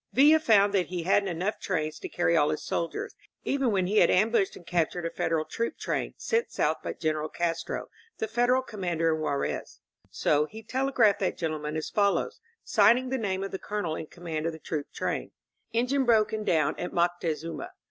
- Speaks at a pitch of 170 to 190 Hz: Yes, medium, 185 Hz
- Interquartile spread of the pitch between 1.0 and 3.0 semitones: No, average, 5.3 semitones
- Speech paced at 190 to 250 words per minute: Yes, average, 200 wpm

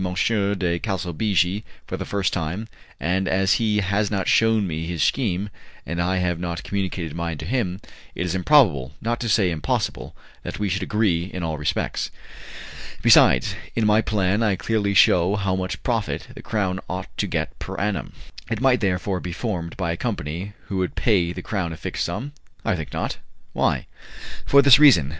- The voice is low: Yes, very low, 95 Hz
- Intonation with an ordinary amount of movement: Yes, average, 3.4 semitones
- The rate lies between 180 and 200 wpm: Yes, average, 185 wpm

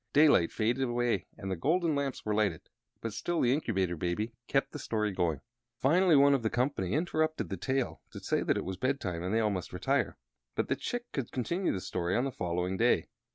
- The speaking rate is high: Yes, fast, 215 wpm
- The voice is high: No, low, 115 Hz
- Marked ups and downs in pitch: Yes, wide, 6.9 semitones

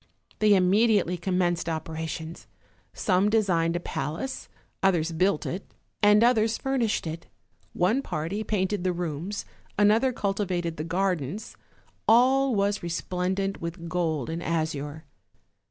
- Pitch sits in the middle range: Yes, medium, 180 Hz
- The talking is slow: Yes, slow, 120 wpm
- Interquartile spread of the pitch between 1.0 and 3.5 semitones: No, average, 3.9 semitones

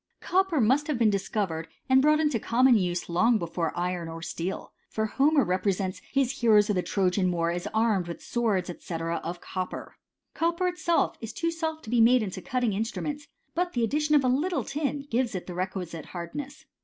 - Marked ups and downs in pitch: Yes, wide, 7.5 semitones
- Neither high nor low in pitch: No, high, 225 Hz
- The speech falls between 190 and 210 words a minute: Yes, average, 195 wpm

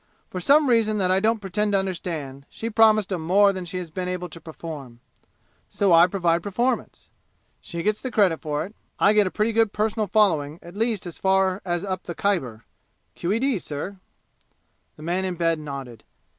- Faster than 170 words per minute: Yes, average, 190 wpm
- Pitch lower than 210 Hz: Yes, medium, 185 Hz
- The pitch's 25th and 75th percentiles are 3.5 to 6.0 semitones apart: Yes, average, 4.0 semitones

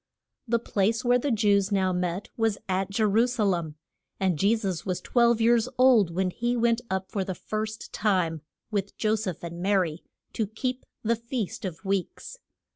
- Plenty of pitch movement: No, average, 3.6 semitones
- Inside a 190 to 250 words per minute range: Yes, average, 195 wpm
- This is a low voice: No, high, 205 Hz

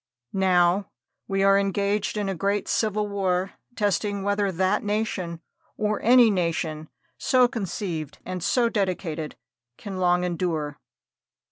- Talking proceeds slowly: Yes, slow, 125 wpm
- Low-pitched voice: No, high, 195 Hz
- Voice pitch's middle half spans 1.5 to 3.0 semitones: Yes, average, 2.7 semitones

